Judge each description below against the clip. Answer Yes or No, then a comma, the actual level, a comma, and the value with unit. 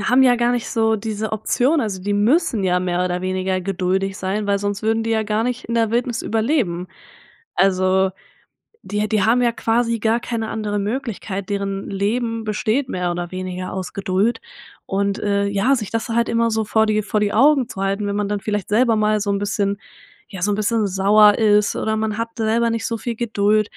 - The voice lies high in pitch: Yes, high, 210 Hz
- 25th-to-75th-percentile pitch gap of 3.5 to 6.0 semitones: No, narrow, 2.5 semitones